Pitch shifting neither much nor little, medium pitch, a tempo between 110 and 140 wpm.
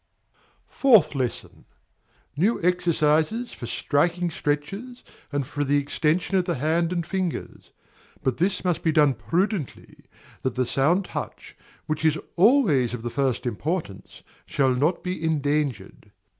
Yes: average, 4.6 semitones; medium, 155 Hz; slow, 135 wpm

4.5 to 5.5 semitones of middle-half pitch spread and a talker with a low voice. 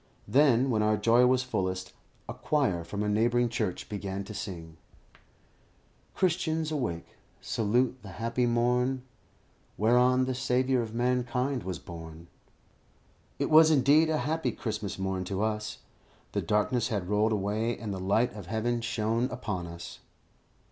No: average, 4.0 semitones; low, 115 Hz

